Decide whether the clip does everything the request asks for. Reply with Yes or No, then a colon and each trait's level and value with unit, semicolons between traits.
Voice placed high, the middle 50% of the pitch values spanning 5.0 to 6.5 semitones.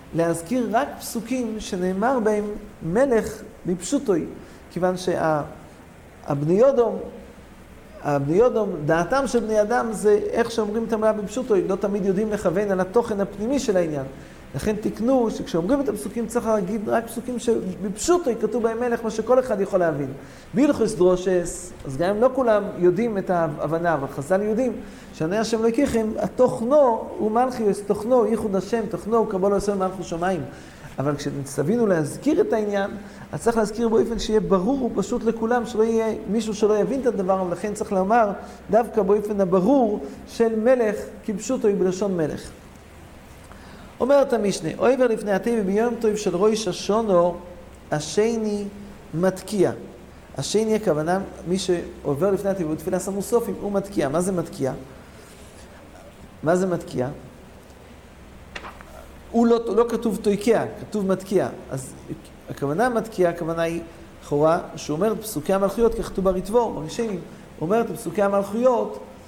No: high, 205 Hz; average, 4.5 semitones